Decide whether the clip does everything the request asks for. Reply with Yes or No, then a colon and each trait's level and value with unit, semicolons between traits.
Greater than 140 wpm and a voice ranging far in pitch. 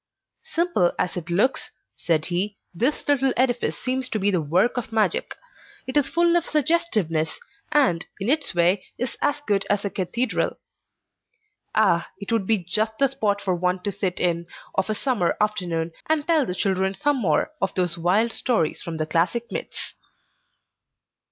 Yes: average, 170 wpm; wide, 6.4 semitones